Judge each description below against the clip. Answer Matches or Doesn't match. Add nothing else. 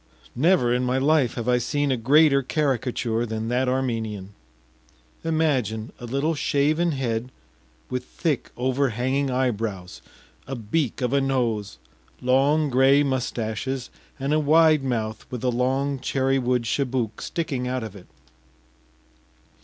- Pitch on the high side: Doesn't match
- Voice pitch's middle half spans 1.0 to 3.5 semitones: Matches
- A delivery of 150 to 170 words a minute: Doesn't match